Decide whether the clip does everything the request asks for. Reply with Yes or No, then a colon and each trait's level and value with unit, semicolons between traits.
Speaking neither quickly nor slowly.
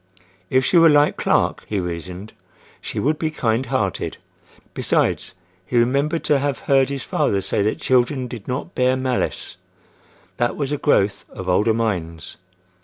Yes: average, 160 wpm